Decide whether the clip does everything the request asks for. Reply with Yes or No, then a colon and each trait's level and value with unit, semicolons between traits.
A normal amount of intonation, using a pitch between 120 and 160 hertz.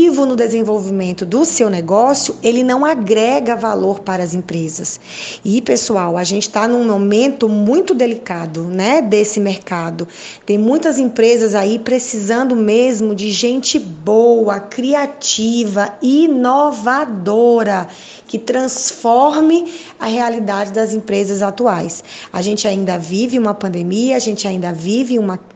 No: average, 3.9 semitones; high, 225 Hz